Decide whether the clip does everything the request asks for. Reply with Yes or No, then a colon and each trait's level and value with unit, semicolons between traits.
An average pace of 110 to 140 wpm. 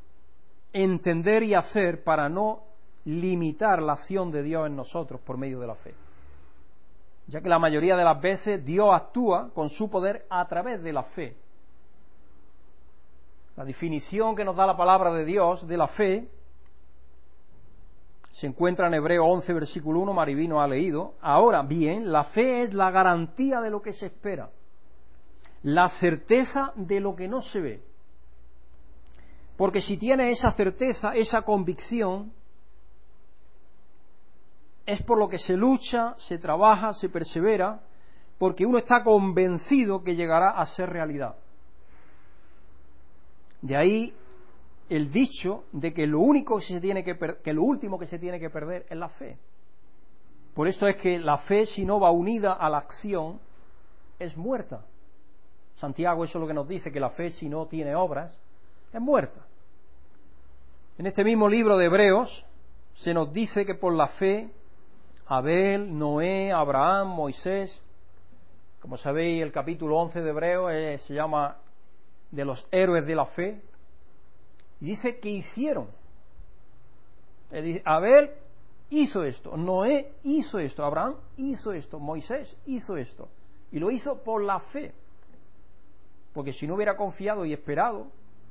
No: average, 150 wpm